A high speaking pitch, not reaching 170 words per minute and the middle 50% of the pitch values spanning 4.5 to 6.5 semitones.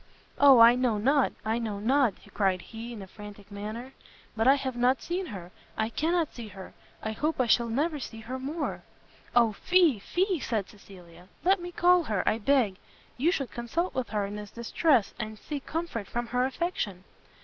No: high, 240 Hz; average, 195 wpm; wide, 5.4 semitones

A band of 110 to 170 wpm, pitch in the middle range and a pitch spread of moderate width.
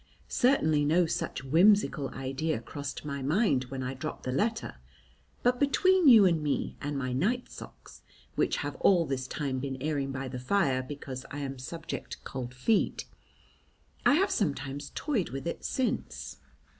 No: average, 165 wpm; medium, 145 Hz; wide, 6.7 semitones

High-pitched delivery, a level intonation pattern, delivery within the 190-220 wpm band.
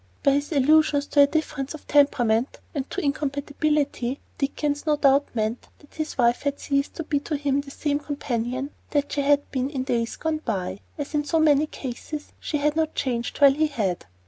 Yes: very high, 285 Hz; narrow, 1.9 semitones; average, 200 wpm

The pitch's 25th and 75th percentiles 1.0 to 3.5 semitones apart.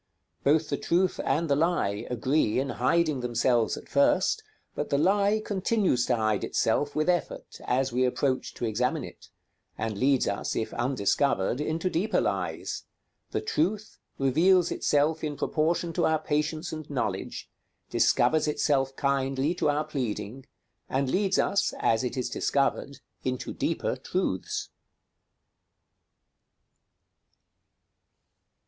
No: average, 4.3 semitones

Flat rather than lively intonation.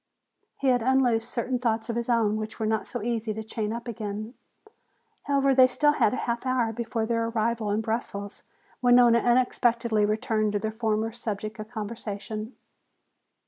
Yes: narrow, 1.9 semitones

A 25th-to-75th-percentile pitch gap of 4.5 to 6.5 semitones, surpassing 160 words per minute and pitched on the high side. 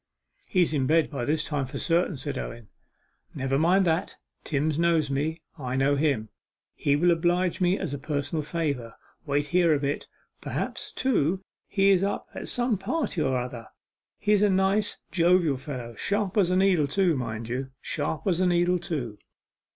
No: average, 4.8 semitones; average, 170 wpm; medium, 160 Hz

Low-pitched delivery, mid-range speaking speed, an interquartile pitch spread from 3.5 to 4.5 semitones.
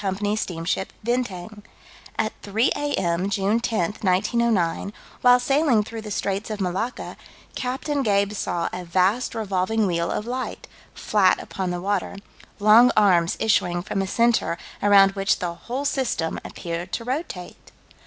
No: high, 205 Hz; average, 145 wpm; average, 4.1 semitones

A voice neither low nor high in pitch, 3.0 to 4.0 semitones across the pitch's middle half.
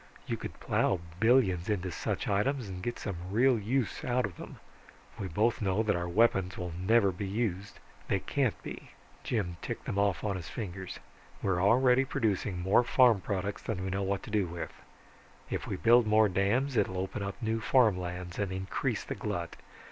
No: low, 100 Hz; average, 3.4 semitones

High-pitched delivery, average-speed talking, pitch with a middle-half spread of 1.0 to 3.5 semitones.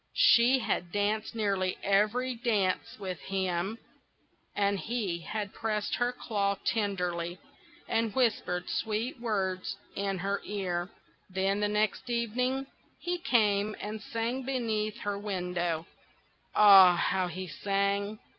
No: high, 205 Hz; slow, 120 wpm; average, 3.1 semitones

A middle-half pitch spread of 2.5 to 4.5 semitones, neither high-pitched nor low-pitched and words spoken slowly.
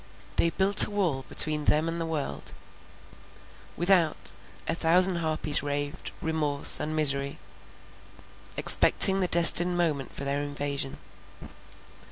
Yes: average, 3.1 semitones; medium, 155 Hz; slow, 115 wpm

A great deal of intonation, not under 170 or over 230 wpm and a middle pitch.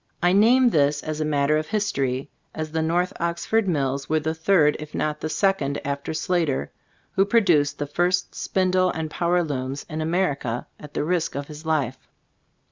No: average, 3.7 semitones; average, 180 wpm; medium, 155 Hz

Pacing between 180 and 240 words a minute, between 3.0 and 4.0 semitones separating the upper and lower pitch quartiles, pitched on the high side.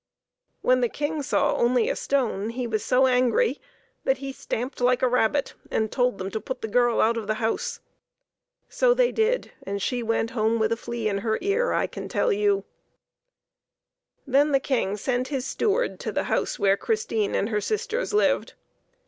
No: average, 190 wpm; average, 5.1 semitones; very high, 250 Hz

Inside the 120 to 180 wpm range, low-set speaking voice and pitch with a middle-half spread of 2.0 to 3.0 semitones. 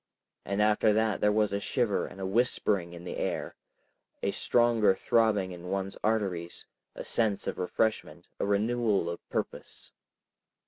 Yes: average, 145 wpm; low, 105 Hz; narrow, 2.6 semitones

